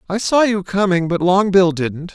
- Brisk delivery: No, average, 195 wpm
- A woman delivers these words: No, male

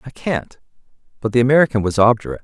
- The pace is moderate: Yes, average, 170 wpm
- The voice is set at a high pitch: No, low, 115 Hz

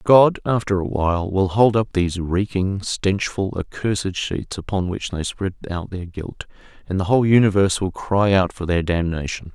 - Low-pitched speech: Yes, very low, 95 Hz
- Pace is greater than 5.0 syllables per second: No, 4.9 syllables/s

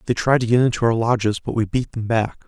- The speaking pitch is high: No, low, 115 Hz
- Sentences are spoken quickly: Yes, fast, 290 wpm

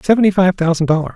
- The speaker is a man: Yes, male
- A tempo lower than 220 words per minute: Yes, fast, 210 wpm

